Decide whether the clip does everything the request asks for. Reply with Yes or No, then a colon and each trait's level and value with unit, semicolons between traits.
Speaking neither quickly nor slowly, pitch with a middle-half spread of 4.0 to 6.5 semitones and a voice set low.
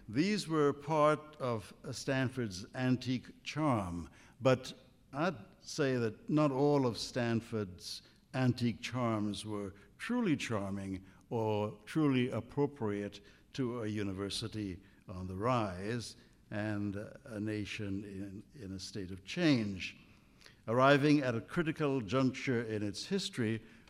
No: slow, 115 wpm; average, 4.6 semitones; low, 115 Hz